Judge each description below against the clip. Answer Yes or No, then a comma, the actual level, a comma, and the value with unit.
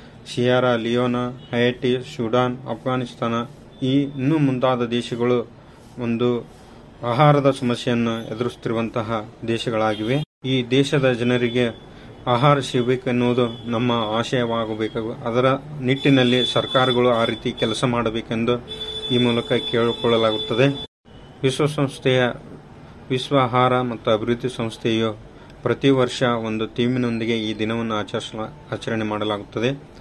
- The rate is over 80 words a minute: Yes, average, 90 wpm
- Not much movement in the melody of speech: Yes, narrow, 2.0 semitones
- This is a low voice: Yes, low, 120 Hz